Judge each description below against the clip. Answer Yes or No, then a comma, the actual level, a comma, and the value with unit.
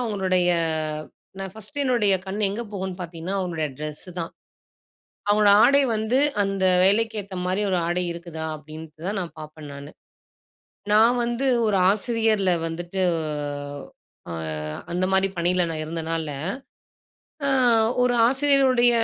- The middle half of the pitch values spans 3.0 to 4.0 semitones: No, average, 4.5 semitones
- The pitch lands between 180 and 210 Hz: Yes, high, 190 Hz